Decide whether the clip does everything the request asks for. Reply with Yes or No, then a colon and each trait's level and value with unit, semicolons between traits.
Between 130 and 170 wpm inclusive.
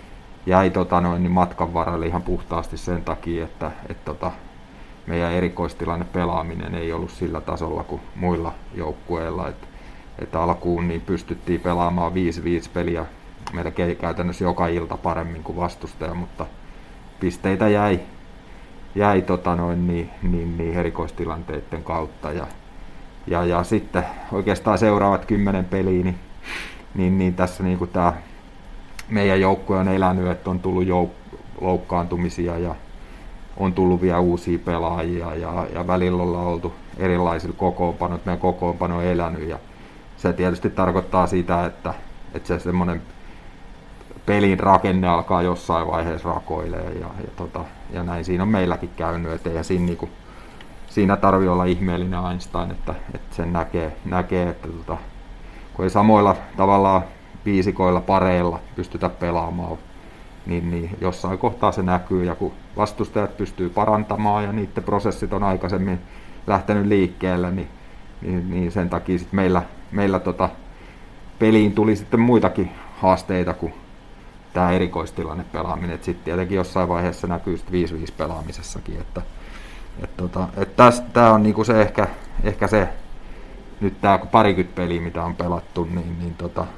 Yes: average, 140 wpm